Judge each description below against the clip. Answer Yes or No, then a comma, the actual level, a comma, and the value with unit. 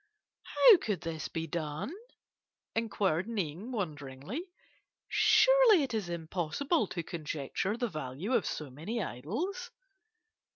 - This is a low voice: No, high, 190 Hz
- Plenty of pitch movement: Yes, wide, 9.0 semitones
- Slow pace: Yes, slow, 115 wpm